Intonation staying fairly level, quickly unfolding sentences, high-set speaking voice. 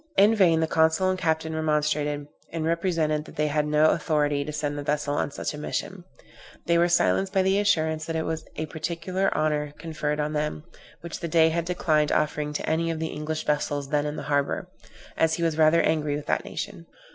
No: narrow, 1.9 semitones; fast, 210 wpm; medium, 155 Hz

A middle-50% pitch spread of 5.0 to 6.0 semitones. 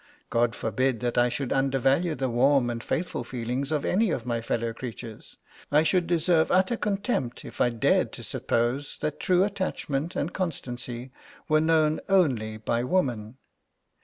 Yes: wide, 5.5 semitones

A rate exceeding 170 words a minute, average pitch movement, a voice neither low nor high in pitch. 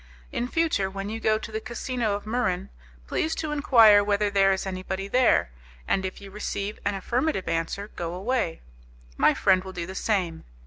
No: average, 185 wpm; average, 3.1 semitones; high, 200 Hz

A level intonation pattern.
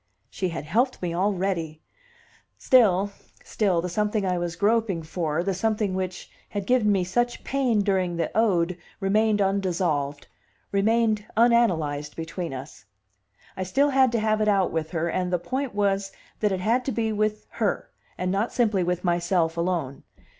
No: average, 3.8 semitones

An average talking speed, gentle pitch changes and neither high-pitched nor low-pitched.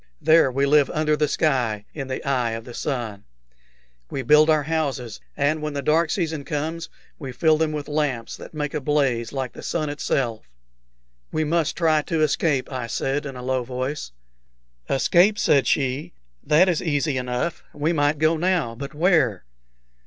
No: average, 175 wpm; average, 3.3 semitones; medium, 145 Hz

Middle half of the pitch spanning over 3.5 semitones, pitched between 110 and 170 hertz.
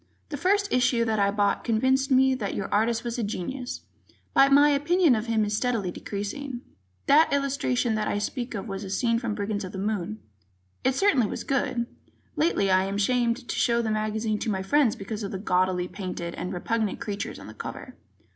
No: average, 4.4 semitones; high, 225 Hz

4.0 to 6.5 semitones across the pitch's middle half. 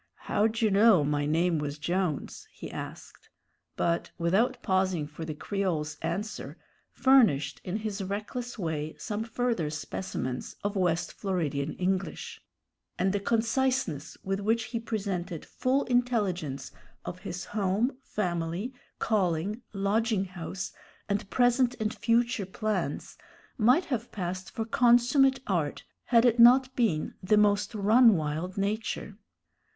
Yes: average, 5.0 semitones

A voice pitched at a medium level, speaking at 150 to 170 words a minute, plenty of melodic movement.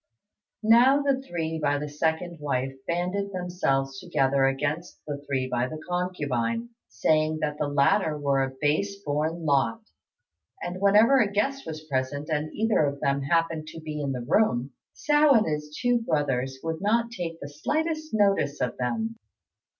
Yes: medium, 155 Hz; average, 165 wpm; wide, 6.1 semitones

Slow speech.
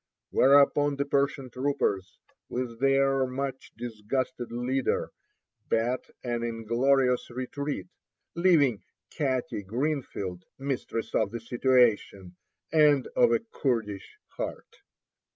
Yes: slow, 100 wpm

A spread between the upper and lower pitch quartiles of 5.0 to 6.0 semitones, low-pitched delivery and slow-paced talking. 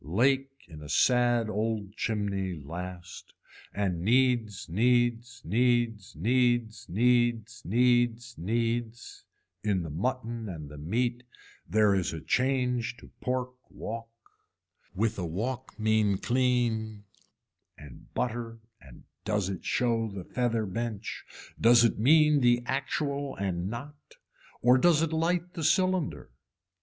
No: average, 3.8 semitones; low, 115 Hz; slow, 125 wpm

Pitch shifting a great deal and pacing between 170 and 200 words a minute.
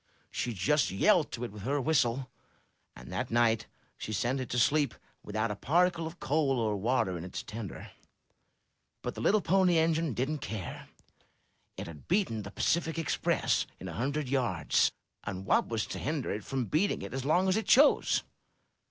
Yes: wide, 6.7 semitones; average, 180 wpm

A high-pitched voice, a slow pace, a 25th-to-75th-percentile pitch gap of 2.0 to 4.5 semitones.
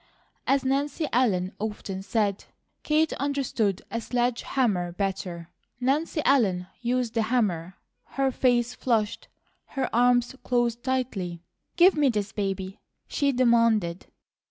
No: high, 235 Hz; slow, 120 wpm; average, 4.9 semitones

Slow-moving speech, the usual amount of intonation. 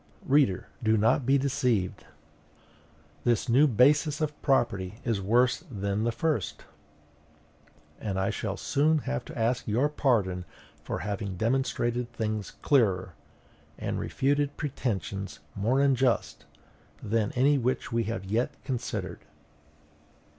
Yes: slow, 120 wpm; average, 4.8 semitones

